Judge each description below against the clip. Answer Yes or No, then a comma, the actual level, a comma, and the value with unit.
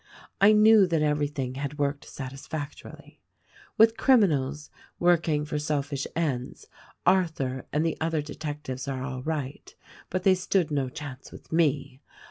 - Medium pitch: Yes, medium, 150 Hz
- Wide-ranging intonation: No, average, 3.3 semitones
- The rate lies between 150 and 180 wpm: No, slow, 135 wpm